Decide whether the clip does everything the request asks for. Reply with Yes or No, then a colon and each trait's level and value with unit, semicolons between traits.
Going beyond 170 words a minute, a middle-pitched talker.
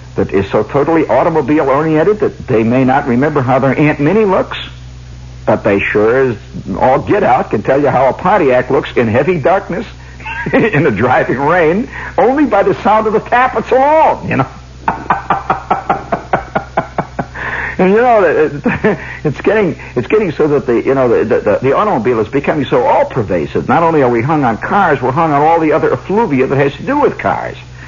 Yes: average, 185 wpm; medium, 155 Hz